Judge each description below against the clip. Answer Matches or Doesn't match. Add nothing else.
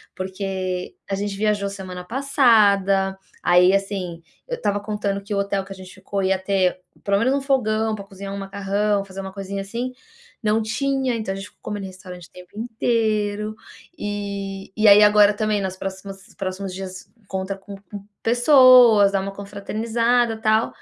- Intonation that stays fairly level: Matches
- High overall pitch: Matches